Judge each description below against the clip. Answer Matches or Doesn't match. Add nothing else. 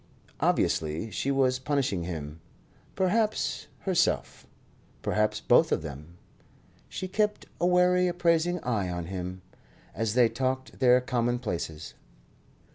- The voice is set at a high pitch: Doesn't match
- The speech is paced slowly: Matches